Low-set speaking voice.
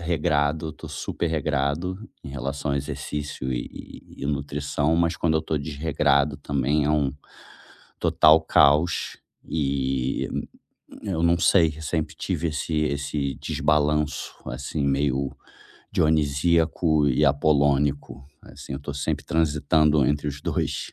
Yes: very low, 75 Hz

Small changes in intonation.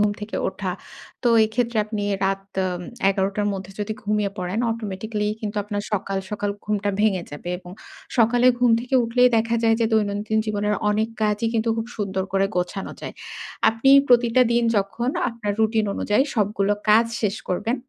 Yes: narrow, 2.3 semitones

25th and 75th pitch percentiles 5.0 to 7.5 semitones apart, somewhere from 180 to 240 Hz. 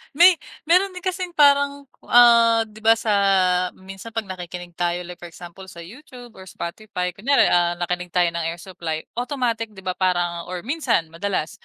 Yes: wide, 5.6 semitones; high, 190 Hz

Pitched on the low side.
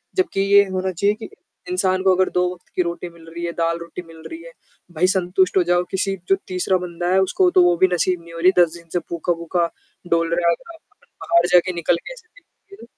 No: medium, 180 Hz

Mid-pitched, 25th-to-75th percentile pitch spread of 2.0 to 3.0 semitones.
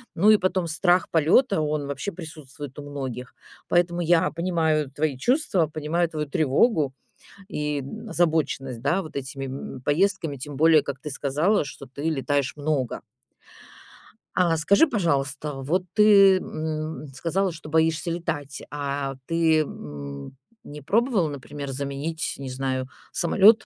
No: medium, 155 Hz; average, 3.7 semitones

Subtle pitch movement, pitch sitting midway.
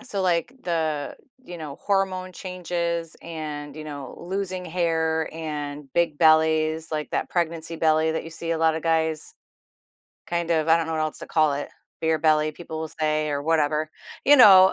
Yes: narrow, 1.7 semitones; medium, 160 Hz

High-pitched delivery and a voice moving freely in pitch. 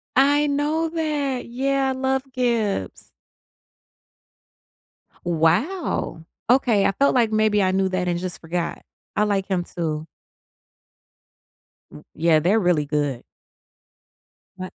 Yes: high, 205 Hz; wide, 7.4 semitones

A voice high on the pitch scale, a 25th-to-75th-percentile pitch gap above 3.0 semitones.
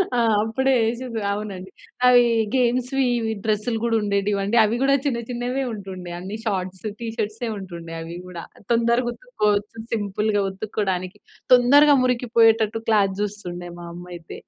Yes: high, 215 Hz; average, 3.7 semitones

